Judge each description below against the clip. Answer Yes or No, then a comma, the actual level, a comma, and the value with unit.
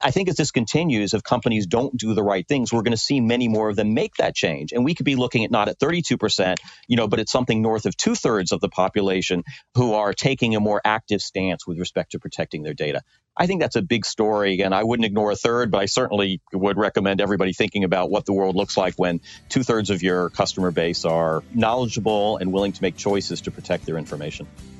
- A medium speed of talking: No, fast, 245 wpm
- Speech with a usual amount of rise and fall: Yes, average, 3.8 semitones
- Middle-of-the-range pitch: No, low, 105 Hz